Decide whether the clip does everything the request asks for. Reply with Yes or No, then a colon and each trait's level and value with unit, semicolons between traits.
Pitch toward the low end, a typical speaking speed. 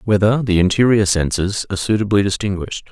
Yes: low, 100 Hz; average, 145 wpm